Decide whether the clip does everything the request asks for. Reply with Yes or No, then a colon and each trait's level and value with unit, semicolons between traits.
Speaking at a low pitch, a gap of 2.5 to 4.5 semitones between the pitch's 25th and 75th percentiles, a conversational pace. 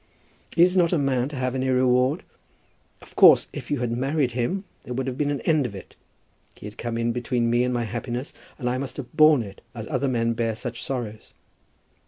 No: low, 125 Hz; average, 2.8 semitones; fast, 220 wpm